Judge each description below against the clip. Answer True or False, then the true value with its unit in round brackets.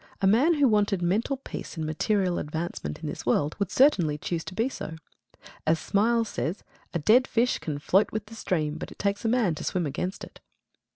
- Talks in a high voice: True (195 Hz)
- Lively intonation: True (5.8 semitones)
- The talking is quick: True (210 wpm)